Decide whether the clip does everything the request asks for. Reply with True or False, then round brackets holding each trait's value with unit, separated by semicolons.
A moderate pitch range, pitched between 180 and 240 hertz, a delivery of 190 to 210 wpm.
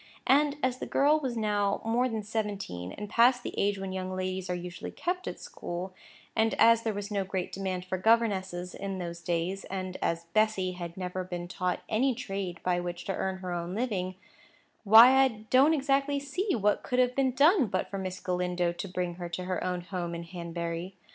True (4.3 semitones; 190 Hz; 205 wpm)